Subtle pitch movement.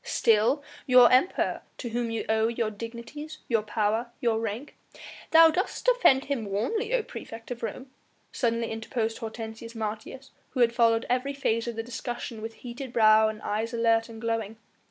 Yes: narrow, 2.1 semitones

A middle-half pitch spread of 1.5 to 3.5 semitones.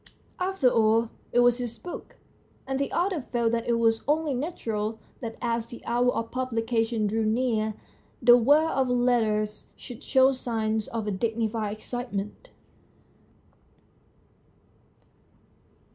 Yes: narrow, 2.4 semitones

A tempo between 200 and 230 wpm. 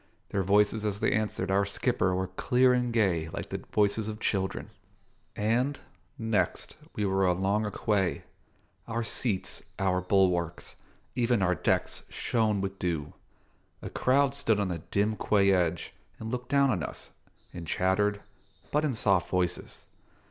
No: average, 155 wpm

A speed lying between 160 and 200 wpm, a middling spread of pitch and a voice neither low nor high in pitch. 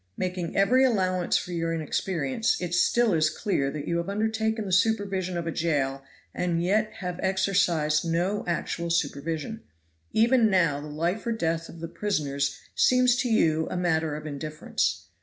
Yes: average, 165 wpm; average, 4.2 semitones; medium, 175 Hz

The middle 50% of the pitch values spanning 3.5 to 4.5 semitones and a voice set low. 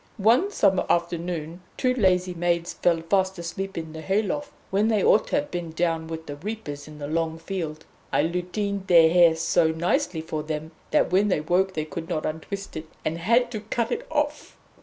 No: average, 3.8 semitones; medium, 175 Hz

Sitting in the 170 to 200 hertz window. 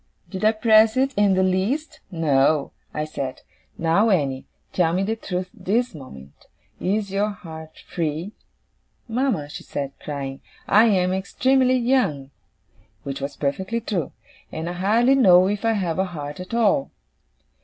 Yes: medium, 185 Hz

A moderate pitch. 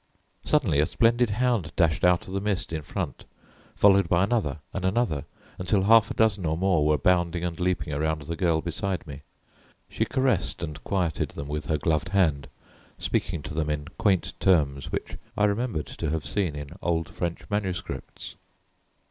No: very low, 85 Hz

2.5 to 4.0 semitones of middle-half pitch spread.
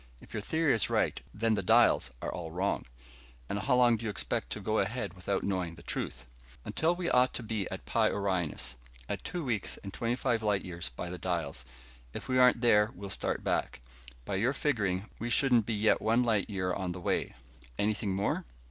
No: average, 4.5 semitones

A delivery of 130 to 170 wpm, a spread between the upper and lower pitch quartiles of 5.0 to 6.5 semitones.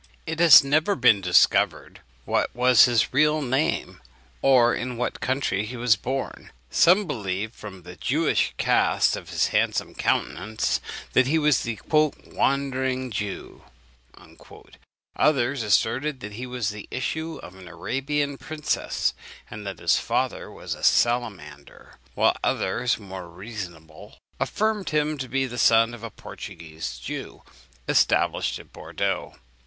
Yes: average, 140 wpm; wide, 5.4 semitones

